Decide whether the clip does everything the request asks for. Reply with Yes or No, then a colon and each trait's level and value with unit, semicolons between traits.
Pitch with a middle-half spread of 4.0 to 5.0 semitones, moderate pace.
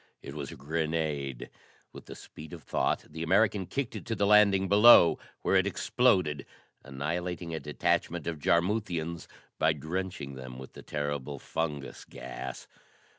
Yes: average, 4.5 semitones; average, 150 wpm